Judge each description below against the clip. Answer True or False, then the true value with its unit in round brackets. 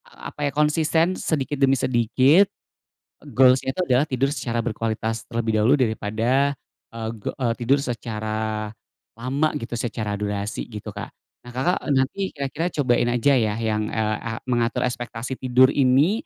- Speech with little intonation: False (3.6 semitones)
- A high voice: False (125 Hz)